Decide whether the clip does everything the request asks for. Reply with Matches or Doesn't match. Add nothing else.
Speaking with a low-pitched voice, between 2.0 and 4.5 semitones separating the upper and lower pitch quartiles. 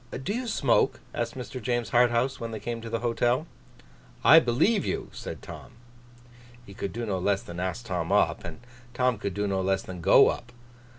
Matches